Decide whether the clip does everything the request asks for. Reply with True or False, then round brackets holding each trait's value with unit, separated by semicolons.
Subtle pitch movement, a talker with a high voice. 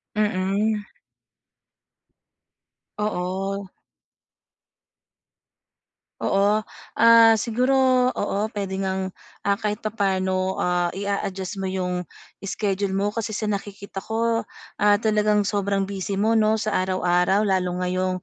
True (2.1 semitones; 200 Hz)